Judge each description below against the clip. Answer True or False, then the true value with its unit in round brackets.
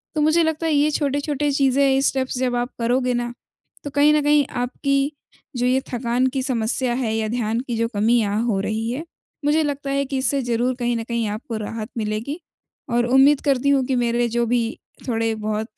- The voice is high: True (250 Hz)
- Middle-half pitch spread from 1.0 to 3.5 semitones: True (3.2 semitones)